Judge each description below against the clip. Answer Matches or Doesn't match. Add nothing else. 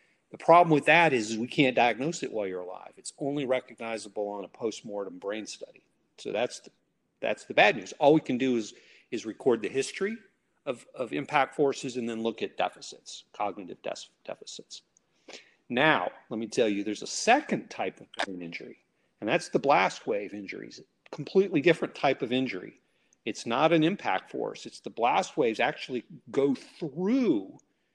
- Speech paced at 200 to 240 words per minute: Doesn't match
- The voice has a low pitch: Matches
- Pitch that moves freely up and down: Matches